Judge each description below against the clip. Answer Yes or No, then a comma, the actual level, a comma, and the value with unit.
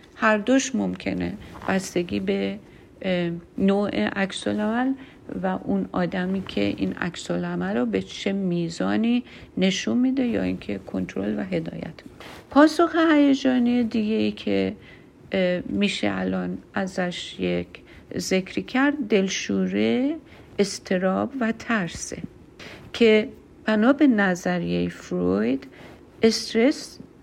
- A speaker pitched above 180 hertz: Yes, high, 190 Hz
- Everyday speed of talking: No, slow, 100 wpm